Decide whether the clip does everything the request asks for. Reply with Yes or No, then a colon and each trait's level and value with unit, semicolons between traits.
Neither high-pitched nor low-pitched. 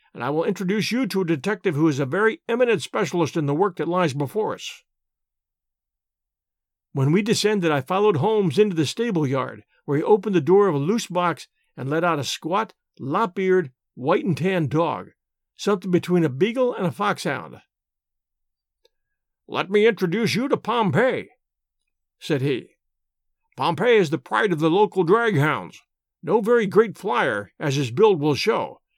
Yes: medium, 180 Hz